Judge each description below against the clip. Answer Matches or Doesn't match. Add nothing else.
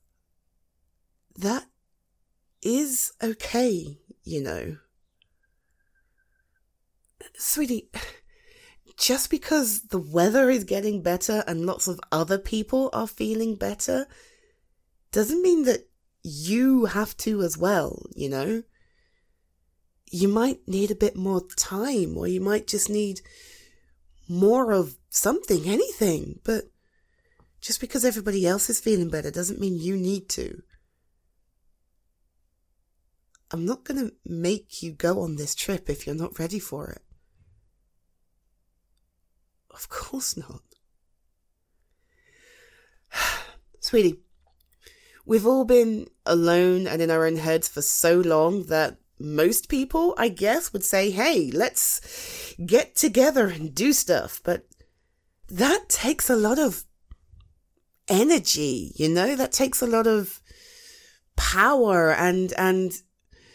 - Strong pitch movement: Matches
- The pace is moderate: Doesn't match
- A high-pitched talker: Matches